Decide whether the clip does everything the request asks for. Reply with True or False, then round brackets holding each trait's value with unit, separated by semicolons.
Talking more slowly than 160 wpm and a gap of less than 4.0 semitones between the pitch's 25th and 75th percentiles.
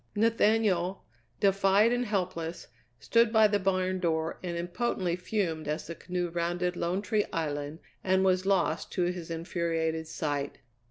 True (145 wpm; 3.0 semitones)